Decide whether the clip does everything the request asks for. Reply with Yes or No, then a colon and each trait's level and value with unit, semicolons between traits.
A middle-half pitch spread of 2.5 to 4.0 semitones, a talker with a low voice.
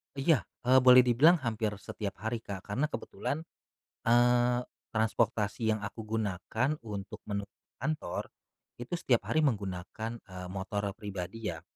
Yes: average, 3.4 semitones; low, 110 Hz